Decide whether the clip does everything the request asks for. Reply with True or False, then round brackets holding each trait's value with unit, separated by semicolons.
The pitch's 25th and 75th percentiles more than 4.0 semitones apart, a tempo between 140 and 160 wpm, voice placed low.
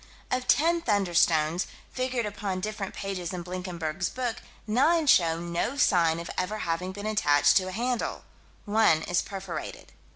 False (4.5 semitones; 150 wpm; 190 Hz)